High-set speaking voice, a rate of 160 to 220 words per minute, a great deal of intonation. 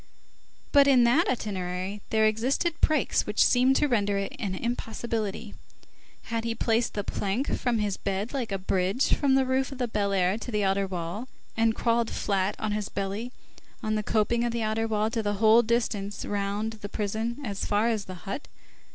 No: high, 220 Hz; average, 190 wpm; average, 3.0 semitones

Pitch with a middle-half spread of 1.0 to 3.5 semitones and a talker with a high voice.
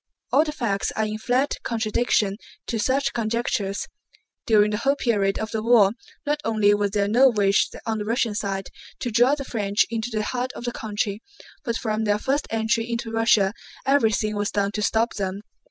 Yes: narrow, 2.5 semitones; high, 220 Hz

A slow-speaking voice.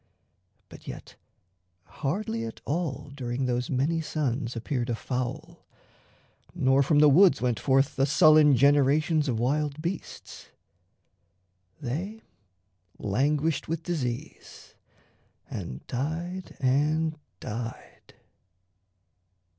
Yes: slow, 100 wpm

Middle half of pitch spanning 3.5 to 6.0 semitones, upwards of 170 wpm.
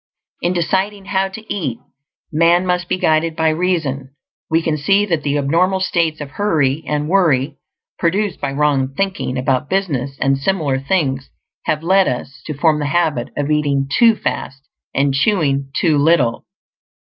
No: average, 4.8 semitones; average, 160 wpm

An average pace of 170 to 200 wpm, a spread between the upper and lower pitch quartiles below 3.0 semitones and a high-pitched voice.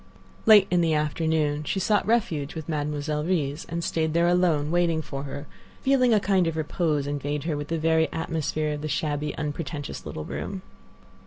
No: average, 180 wpm; narrow, 2.5 semitones; medium, 155 Hz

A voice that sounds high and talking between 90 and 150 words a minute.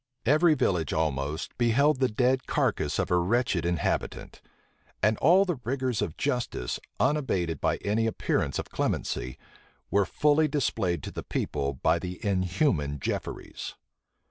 No: low, 105 Hz; average, 140 wpm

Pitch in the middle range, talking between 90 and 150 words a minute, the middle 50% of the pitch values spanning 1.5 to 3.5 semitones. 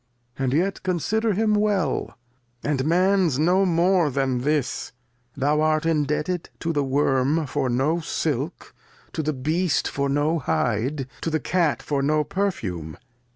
No: medium, 155 Hz; average, 145 wpm; average, 4.1 semitones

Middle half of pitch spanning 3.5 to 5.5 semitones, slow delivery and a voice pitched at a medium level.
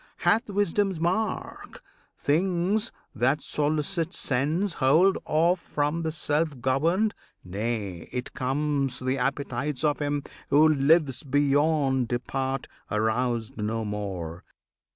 Yes: average, 4.6 semitones; slow, 110 wpm; medium, 145 Hz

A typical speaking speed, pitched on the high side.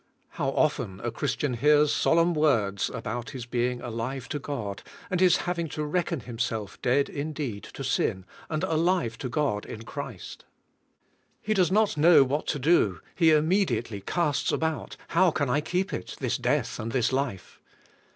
No: average, 165 wpm; medium, 140 Hz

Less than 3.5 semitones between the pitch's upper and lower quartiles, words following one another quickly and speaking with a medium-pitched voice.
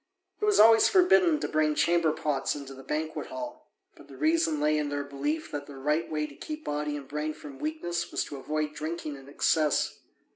Yes: average, 3.0 semitones; fast, 210 wpm; medium, 155 Hz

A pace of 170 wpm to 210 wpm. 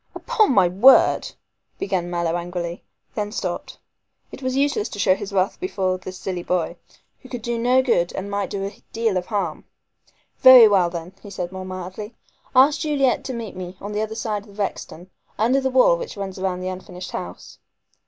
Yes: average, 195 wpm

